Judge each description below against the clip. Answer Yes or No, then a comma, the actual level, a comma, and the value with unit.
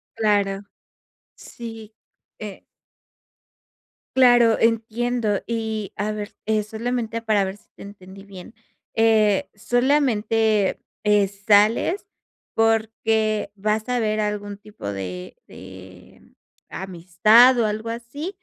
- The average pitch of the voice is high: Yes, high, 215 Hz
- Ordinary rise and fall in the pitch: No, narrow, 2.1 semitones